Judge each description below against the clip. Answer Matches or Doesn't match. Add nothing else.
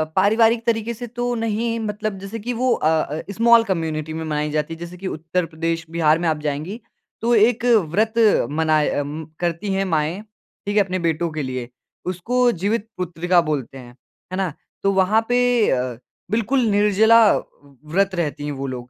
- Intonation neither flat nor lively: Doesn't match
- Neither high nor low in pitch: Matches